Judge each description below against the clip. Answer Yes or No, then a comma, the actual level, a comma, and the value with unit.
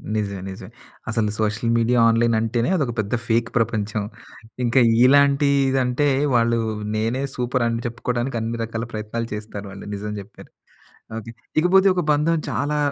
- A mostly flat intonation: No, average, 3.2 semitones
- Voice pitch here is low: Yes, low, 115 Hz